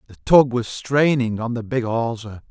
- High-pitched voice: No, low, 120 Hz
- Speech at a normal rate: Yes, average, 190 wpm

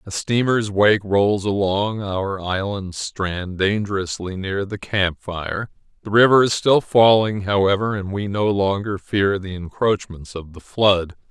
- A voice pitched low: Yes, low, 100 Hz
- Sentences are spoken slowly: No, average, 155 wpm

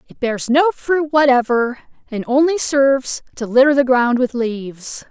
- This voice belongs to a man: No, female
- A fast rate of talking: No, average, 165 wpm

